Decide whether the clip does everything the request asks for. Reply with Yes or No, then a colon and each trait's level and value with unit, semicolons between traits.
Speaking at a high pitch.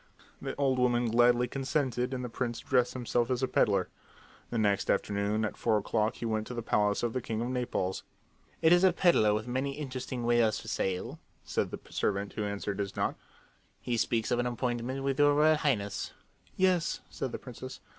No: low, 120 Hz